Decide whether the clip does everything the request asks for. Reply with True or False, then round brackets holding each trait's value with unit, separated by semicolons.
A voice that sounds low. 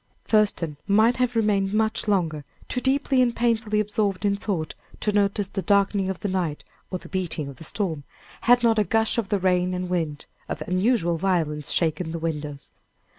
False (195 Hz)